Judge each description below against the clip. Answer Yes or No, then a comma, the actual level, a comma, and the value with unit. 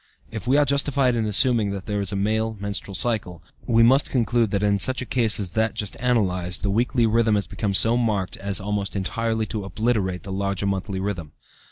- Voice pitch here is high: No, low, 105 Hz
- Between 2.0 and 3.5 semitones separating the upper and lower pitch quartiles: Yes, average, 2.9 semitones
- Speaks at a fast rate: Yes, fast, 210 wpm